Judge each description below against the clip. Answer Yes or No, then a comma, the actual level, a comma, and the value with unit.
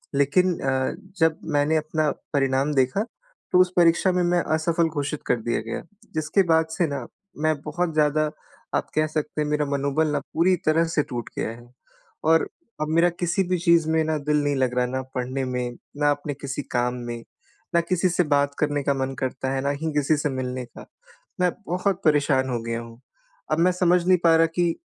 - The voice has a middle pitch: Yes, medium, 150 Hz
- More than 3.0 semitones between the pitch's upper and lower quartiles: Yes, average, 3.9 semitones